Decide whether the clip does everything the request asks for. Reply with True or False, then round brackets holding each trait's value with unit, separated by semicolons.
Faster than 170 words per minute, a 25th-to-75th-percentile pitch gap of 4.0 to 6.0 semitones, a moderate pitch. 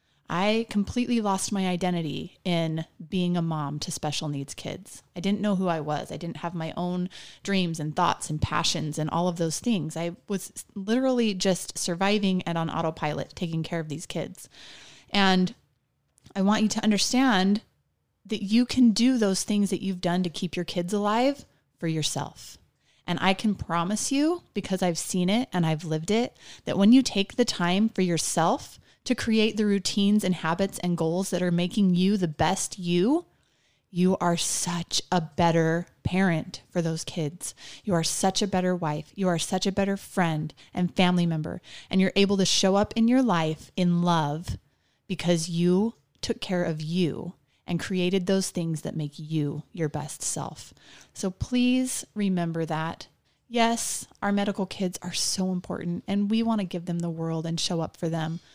False (185 wpm; 3.4 semitones; 180 Hz)